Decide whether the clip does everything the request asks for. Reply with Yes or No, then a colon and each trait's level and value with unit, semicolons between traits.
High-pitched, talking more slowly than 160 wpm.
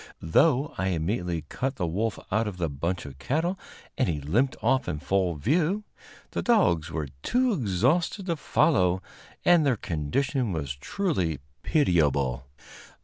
No: very low, 95 Hz; average, 145 wpm